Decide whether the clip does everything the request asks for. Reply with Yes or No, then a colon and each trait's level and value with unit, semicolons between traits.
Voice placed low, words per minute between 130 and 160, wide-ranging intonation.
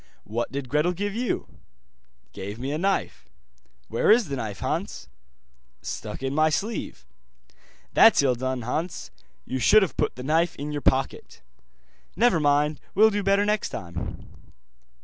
No: medium, 150 Hz; average, 150 wpm; wide, 7.1 semitones